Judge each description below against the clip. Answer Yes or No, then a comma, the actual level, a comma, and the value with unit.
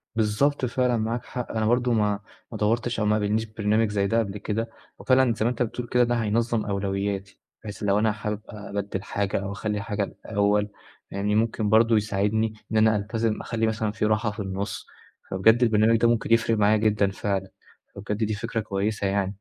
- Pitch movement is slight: Yes, narrow, 1.9 semitones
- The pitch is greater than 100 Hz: Yes, low, 110 Hz